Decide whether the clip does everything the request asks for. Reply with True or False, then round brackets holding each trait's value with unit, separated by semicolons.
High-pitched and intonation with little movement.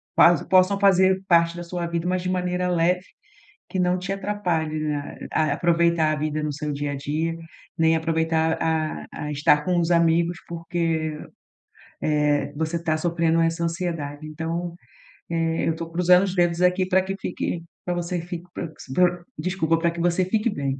False (170 Hz; 2.0 semitones)